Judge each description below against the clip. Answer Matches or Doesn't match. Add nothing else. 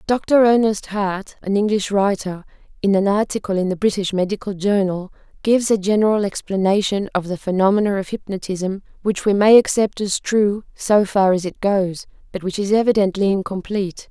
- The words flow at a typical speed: Matches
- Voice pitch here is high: Matches